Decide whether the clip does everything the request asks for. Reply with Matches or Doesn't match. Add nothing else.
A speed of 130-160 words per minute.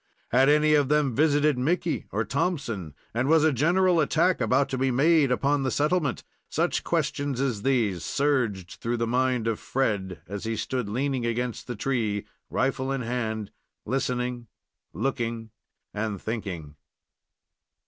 Matches